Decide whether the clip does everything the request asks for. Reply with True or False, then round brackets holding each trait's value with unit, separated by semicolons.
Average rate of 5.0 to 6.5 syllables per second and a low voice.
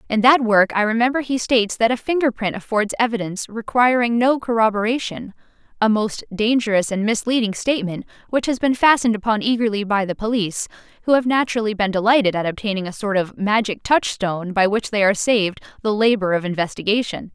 False (6.2 syllables/s; 220 Hz)